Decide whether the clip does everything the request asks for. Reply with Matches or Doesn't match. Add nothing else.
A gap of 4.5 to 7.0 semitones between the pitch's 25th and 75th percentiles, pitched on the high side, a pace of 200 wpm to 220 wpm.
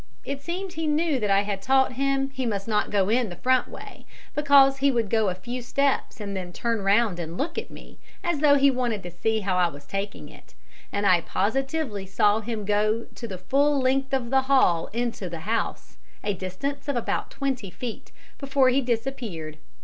Matches